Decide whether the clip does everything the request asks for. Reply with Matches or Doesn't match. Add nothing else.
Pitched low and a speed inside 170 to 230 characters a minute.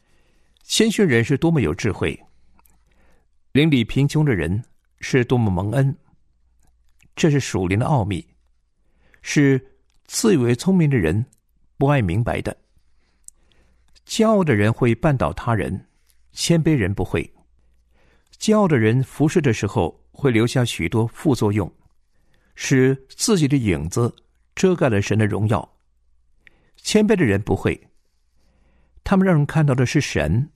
Matches